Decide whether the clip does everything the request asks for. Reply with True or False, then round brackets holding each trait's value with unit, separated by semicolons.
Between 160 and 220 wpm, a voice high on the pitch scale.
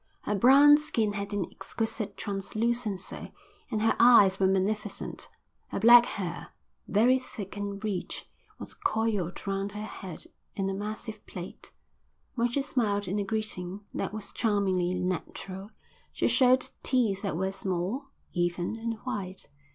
False (145 wpm; 205 Hz)